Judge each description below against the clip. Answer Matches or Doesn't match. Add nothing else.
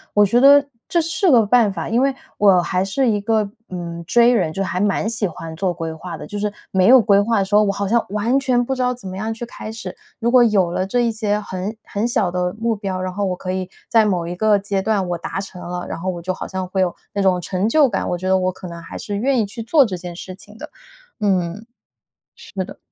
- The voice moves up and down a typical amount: Matches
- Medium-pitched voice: Doesn't match